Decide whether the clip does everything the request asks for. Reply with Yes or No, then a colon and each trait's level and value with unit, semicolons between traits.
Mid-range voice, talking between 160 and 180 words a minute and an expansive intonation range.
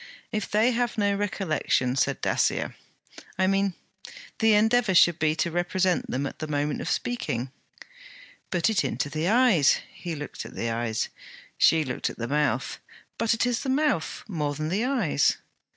Yes: medium, 175 Hz; average, 170 wpm; wide, 7.0 semitones